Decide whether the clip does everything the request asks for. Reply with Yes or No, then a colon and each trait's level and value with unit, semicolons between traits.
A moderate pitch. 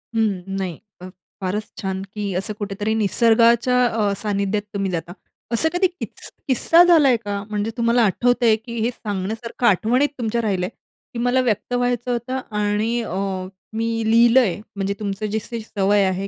No: high, 220 Hz